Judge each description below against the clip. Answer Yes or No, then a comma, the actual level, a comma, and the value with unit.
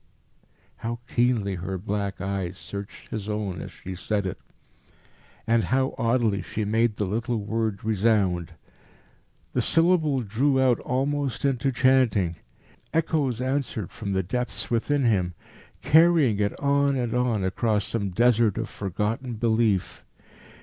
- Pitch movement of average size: Yes, average, 4.2 semitones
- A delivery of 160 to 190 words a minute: No, slow, 135 wpm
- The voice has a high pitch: No, low, 115 Hz